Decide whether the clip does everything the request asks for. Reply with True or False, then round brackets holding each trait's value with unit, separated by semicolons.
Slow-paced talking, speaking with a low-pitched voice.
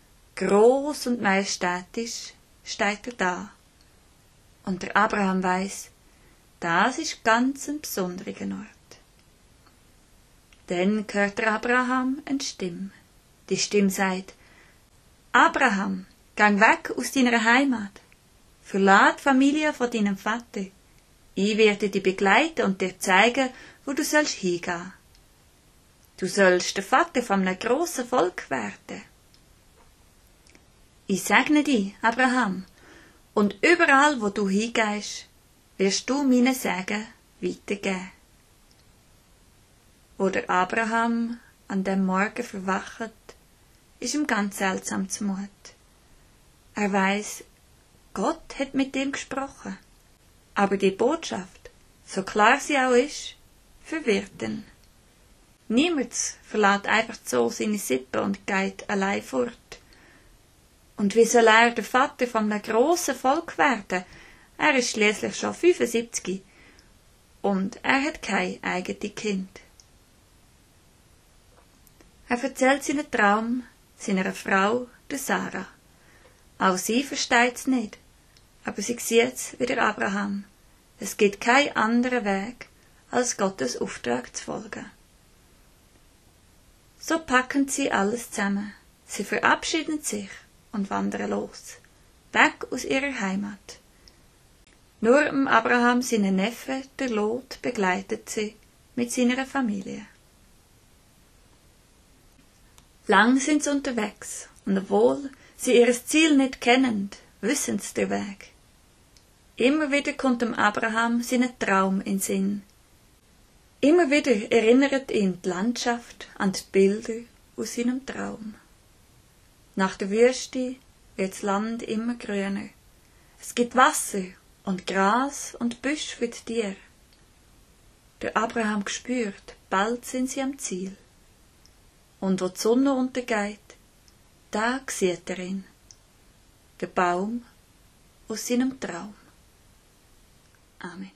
False (110 wpm; 220 Hz)